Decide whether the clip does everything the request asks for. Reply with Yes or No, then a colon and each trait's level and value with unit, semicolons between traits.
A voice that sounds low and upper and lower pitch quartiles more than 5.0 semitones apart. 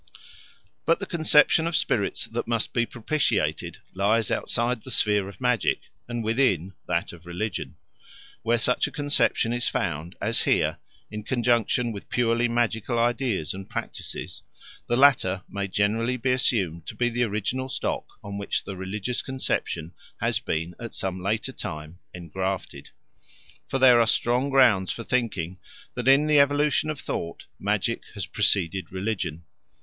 No: low, 115 Hz; average, 4.7 semitones